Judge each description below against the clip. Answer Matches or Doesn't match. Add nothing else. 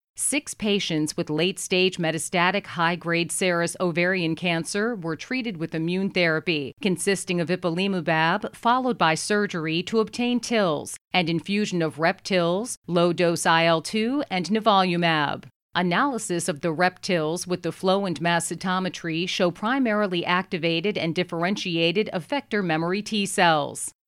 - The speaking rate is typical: Doesn't match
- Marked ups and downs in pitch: Doesn't match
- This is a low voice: Doesn't match